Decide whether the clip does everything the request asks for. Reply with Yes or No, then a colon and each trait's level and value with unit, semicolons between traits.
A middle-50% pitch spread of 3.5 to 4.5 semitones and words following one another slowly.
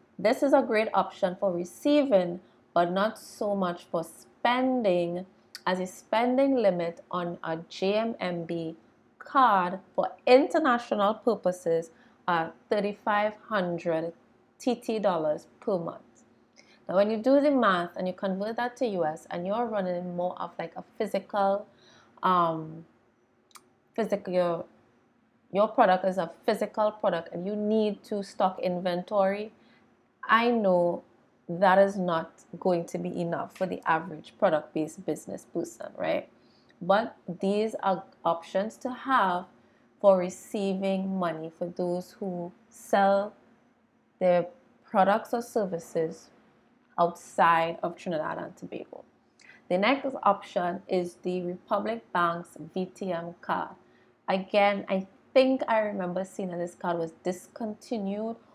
Yes: average, 3.9 semitones; slow, 130 wpm